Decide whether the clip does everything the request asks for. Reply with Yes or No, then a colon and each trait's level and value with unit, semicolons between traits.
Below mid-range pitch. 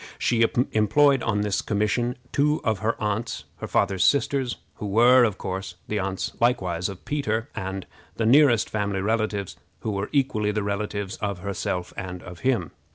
Yes: low, 105 Hz